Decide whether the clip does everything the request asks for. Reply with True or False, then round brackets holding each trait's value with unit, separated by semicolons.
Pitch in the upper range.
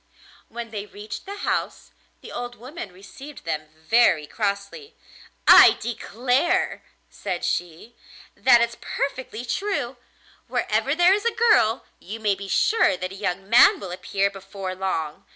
True (220 Hz)